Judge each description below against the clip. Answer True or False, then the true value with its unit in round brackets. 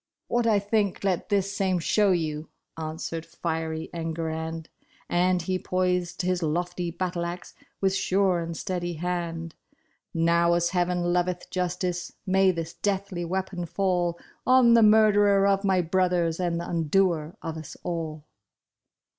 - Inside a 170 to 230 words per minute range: False (145 wpm)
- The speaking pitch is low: False (175 Hz)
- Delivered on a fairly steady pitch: True (2.2 semitones)